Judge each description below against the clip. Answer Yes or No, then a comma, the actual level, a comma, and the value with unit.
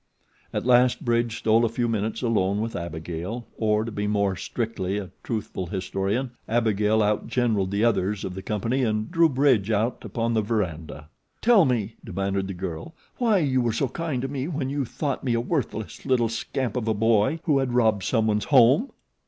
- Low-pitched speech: Yes, low, 115 Hz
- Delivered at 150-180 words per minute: No, average, 190 wpm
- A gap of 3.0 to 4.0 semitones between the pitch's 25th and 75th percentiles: Yes, average, 3.7 semitones